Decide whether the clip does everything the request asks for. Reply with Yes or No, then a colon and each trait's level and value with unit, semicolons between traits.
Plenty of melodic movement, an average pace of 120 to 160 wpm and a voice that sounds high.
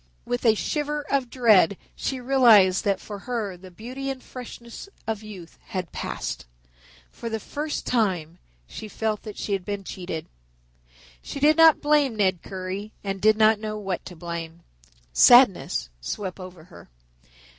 No: average, 4.9 semitones; average, 155 wpm; high, 210 Hz